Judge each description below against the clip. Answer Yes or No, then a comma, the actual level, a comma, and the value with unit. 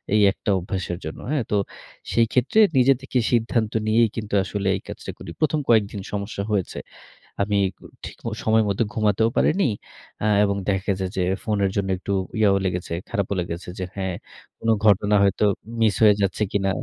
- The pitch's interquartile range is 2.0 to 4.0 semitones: Yes, narrow, 2.5 semitones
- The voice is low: Yes, low, 105 Hz